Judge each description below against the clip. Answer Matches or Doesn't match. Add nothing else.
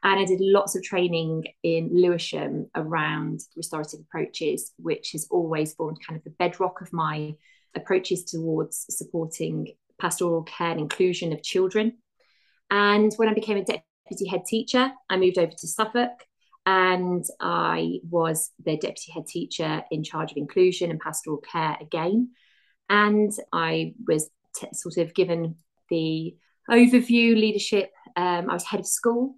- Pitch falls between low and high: Matches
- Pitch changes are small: Doesn't match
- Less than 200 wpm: Matches